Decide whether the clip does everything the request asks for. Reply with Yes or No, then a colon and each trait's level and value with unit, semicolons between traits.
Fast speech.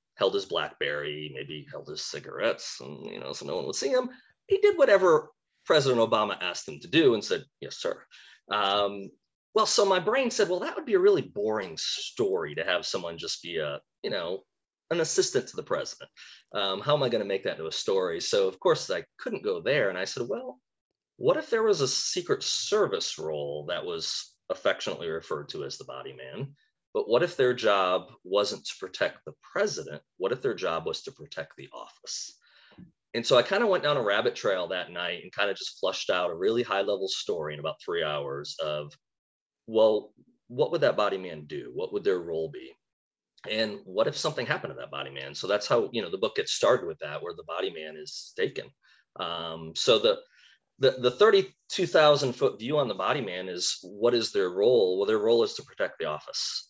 Yes: fast, 215 wpm